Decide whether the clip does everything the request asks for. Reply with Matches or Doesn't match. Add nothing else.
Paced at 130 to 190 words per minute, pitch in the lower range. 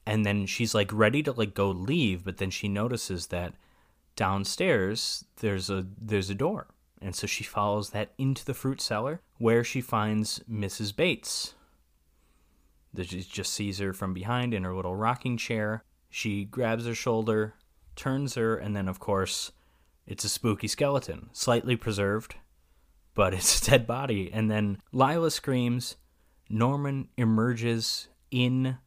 Matches